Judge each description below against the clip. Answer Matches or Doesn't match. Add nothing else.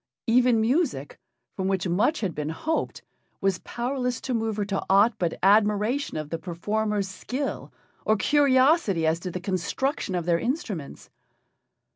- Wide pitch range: Matches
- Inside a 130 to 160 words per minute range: Matches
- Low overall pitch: Doesn't match